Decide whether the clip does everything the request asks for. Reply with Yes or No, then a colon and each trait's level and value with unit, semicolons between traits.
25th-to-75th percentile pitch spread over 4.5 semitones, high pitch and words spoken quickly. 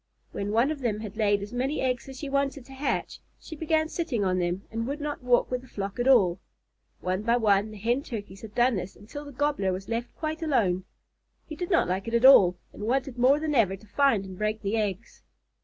Yes: wide, 5.4 semitones; high, 235 Hz; fast, 240 wpm